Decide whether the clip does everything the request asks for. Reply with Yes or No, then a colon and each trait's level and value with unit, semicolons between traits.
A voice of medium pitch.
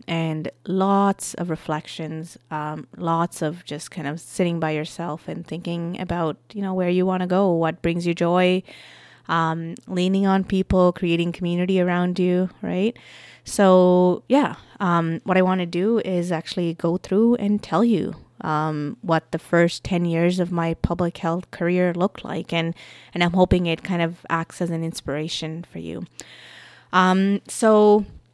Yes: medium, 175 Hz